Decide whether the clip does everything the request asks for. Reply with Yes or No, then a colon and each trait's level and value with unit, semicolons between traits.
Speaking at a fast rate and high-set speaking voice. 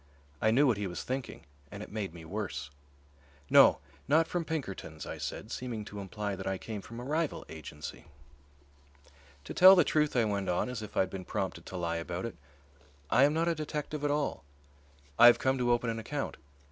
No: fast, 210 wpm; low, 115 Hz